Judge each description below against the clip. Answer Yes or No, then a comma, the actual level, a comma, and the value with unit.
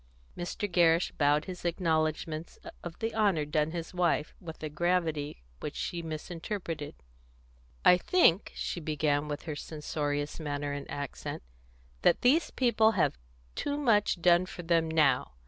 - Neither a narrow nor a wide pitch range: Yes, average, 3.1 semitones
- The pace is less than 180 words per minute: Yes, average, 145 wpm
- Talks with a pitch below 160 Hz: No, medium, 165 Hz